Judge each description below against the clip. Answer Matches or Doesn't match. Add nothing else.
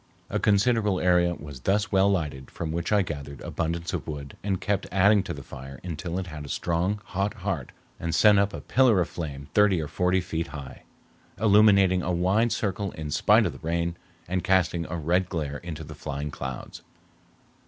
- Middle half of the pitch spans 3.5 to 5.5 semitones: Matches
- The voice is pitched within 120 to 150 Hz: Doesn't match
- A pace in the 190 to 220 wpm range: Matches